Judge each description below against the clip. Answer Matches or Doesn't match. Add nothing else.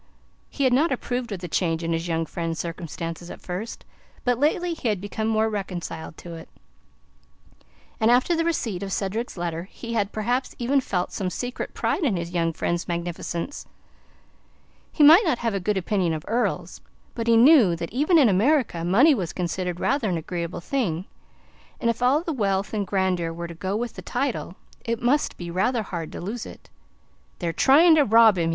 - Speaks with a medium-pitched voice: Doesn't match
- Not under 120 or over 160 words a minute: Doesn't match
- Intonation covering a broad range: Matches